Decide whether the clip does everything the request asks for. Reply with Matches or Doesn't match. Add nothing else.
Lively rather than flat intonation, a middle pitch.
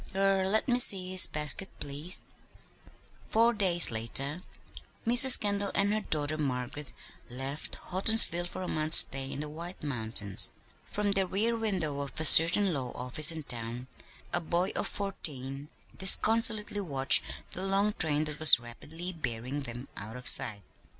Matches